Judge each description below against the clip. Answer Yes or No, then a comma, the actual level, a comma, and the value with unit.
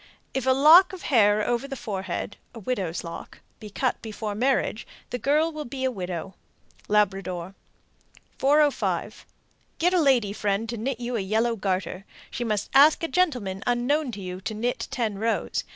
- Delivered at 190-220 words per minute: No, average, 170 wpm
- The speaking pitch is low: No, high, 230 Hz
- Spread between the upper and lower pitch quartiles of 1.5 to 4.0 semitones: No, average, 5.2 semitones